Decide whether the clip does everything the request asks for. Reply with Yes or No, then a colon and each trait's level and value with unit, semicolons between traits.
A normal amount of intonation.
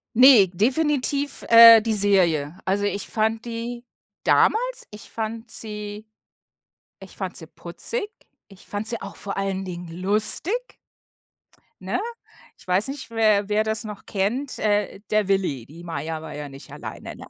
Yes: average, 3.3 semitones